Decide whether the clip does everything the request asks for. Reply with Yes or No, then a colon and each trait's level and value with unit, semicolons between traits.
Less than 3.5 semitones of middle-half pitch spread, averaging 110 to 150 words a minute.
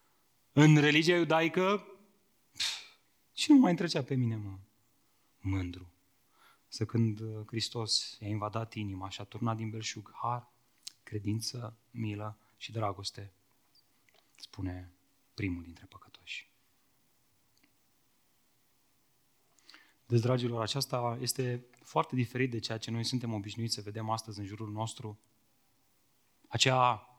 Yes: average, 3.1 semitones; slow, 115 wpm